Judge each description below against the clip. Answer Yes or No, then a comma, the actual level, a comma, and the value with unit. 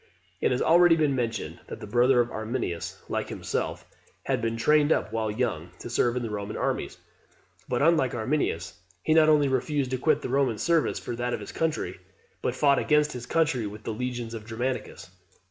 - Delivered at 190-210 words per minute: Yes, average, 195 wpm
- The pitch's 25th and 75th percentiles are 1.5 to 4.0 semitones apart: No, average, 4.6 semitones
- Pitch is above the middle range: No, low, 125 Hz